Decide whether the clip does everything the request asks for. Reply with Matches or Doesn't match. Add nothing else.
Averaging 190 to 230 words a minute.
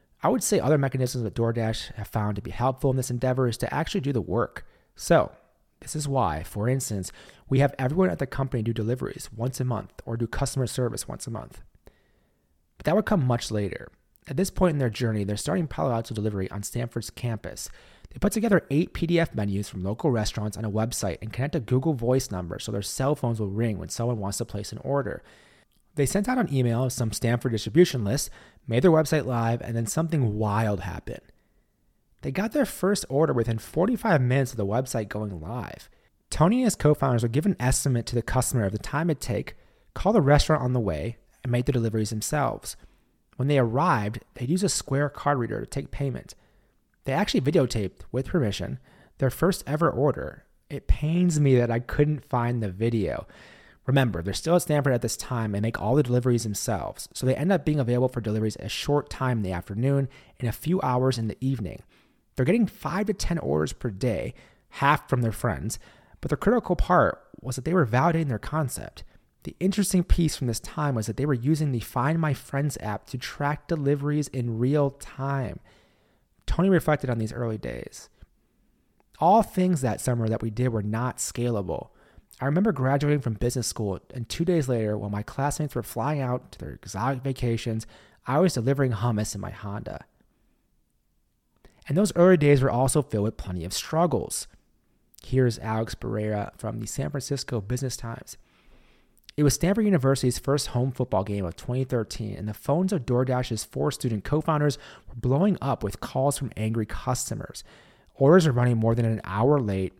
Matches